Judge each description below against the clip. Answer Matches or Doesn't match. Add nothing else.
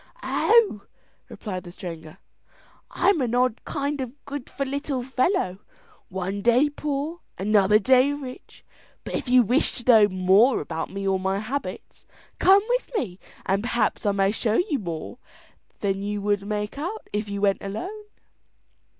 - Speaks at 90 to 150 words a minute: Doesn't match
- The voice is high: Matches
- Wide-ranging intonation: Matches